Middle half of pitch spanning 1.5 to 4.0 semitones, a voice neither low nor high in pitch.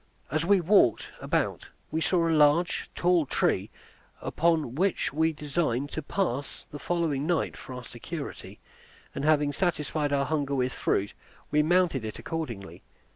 Yes: average, 3.4 semitones; medium, 150 Hz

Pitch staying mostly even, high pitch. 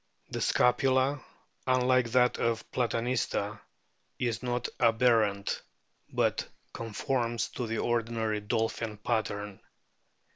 No: narrow, 2.1 semitones; low, 115 Hz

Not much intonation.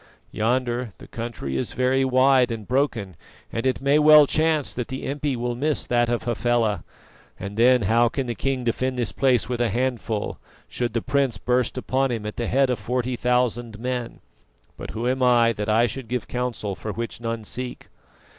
Yes: narrow, 2.0 semitones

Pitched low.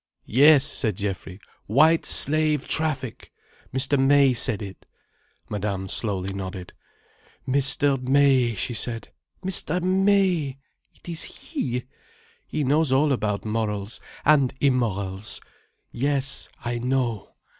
Yes: low, 130 Hz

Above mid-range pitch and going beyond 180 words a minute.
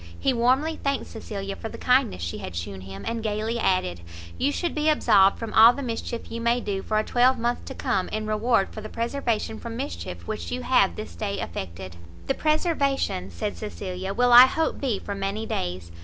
Yes: high, 220 Hz; average, 200 wpm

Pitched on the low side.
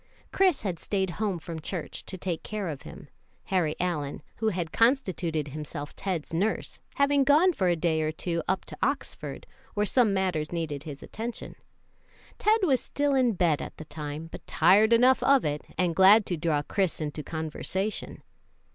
No: medium, 185 Hz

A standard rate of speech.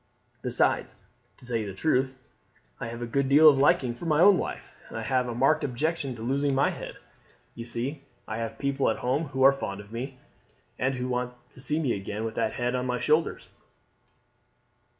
No: fast, 210 wpm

